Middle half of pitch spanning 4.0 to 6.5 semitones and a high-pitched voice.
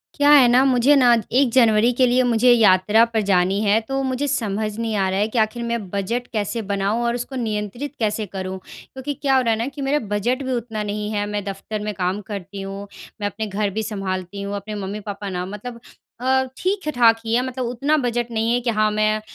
No: average, 3.4 semitones; high, 220 Hz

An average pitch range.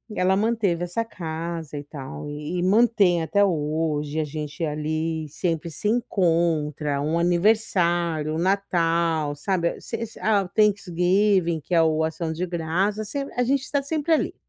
Yes: average, 4.1 semitones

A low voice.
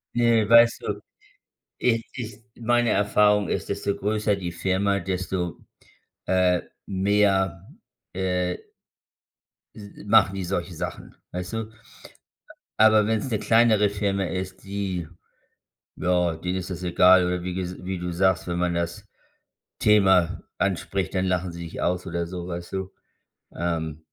Yes: very low, 95 Hz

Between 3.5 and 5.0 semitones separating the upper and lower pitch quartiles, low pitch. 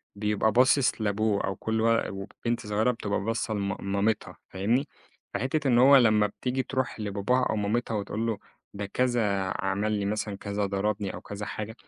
No: average, 2.8 semitones; low, 105 Hz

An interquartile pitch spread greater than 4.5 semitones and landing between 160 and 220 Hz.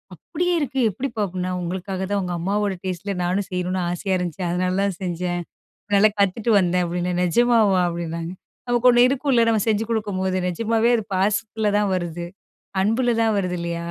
No: average, 3.7 semitones; high, 190 Hz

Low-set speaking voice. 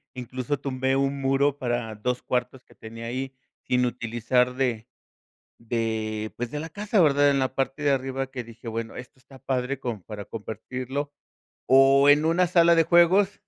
Yes: low, 130 Hz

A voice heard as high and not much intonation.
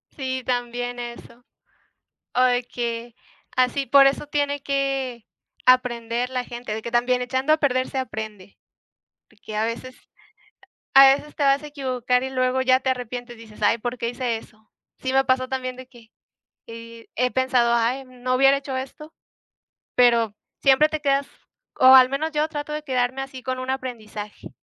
Yes: very high, 255 Hz; narrow, 2.1 semitones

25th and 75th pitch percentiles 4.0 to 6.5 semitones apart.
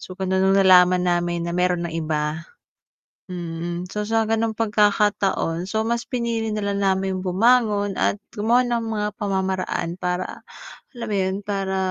No: average, 3.0 semitones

